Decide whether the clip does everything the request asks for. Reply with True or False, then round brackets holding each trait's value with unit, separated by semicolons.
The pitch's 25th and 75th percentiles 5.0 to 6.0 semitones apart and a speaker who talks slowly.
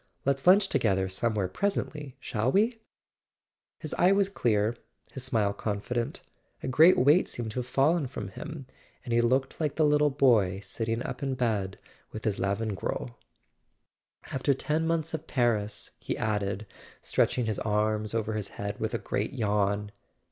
False (5.5 semitones; 160 wpm)